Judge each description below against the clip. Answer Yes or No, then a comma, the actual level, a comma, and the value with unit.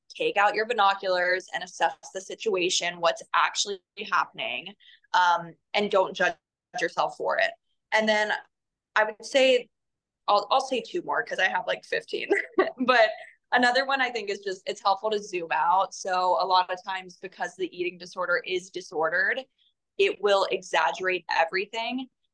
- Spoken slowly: No, average, 160 wpm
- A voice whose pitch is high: Yes, high, 200 Hz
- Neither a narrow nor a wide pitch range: No, wide, 6.2 semitones